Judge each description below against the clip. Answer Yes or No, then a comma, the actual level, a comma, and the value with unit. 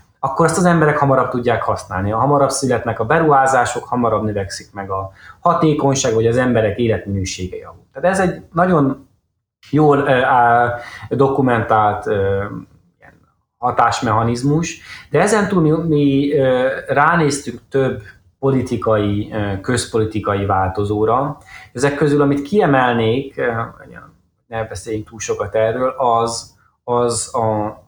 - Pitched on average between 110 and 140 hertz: Yes, low, 120 Hz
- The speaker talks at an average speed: Yes, average, 120 wpm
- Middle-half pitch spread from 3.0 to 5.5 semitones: Yes, average, 4.6 semitones